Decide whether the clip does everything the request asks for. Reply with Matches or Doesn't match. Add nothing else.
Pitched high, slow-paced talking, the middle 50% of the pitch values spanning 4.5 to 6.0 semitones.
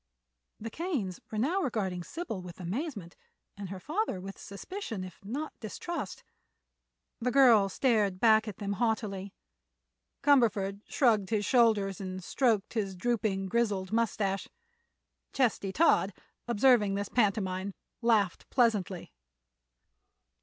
Doesn't match